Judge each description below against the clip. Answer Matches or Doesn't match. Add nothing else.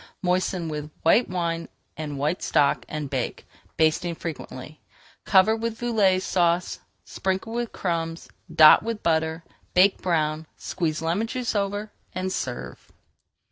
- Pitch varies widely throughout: Doesn't match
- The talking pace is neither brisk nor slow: Doesn't match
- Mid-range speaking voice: Matches